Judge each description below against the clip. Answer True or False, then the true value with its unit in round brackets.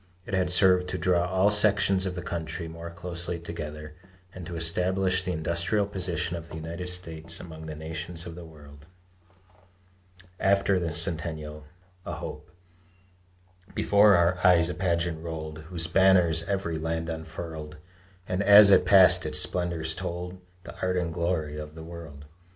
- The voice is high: False (85 Hz)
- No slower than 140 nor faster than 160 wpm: True (155 wpm)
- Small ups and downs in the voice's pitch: True (2.2 semitones)